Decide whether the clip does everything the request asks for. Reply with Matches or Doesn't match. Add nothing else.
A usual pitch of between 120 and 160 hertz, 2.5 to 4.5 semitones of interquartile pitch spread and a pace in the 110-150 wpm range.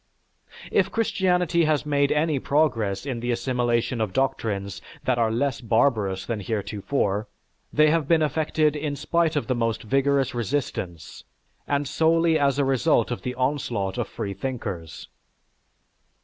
Doesn't match